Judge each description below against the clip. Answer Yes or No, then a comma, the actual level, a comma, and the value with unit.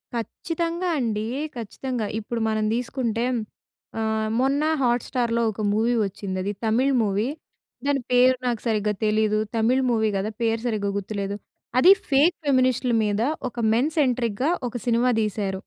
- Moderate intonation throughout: Yes, average, 3.0 semitones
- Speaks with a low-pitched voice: No, high, 230 Hz